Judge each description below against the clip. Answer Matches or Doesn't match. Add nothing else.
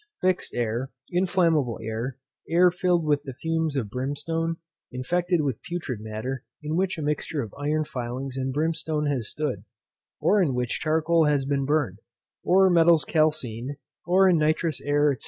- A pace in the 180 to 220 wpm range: Doesn't match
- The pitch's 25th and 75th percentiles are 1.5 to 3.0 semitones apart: Doesn't match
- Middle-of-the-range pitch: Matches